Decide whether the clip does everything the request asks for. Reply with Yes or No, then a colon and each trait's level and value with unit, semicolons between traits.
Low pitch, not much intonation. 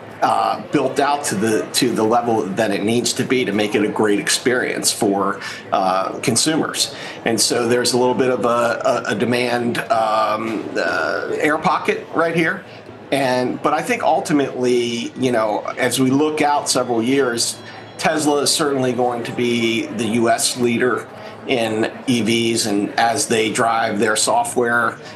Yes: low, 120 Hz; narrow, 2.3 semitones